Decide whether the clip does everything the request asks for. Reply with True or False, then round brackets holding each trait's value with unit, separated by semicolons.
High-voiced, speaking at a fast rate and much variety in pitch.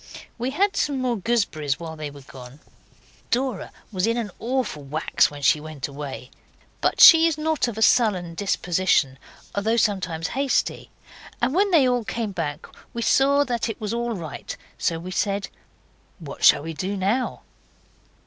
False (200 Hz; 165 wpm; 7.4 semitones)